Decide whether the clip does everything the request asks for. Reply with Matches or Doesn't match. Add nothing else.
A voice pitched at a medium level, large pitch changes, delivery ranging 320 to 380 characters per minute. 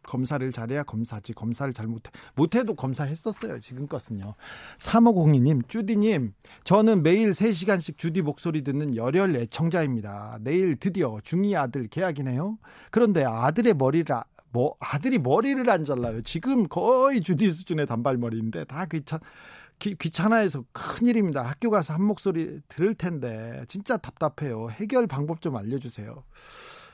Matches